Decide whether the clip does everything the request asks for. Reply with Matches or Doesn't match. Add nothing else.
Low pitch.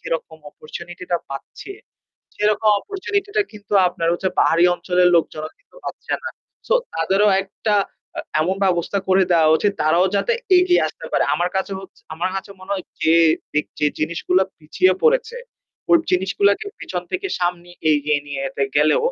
Doesn't match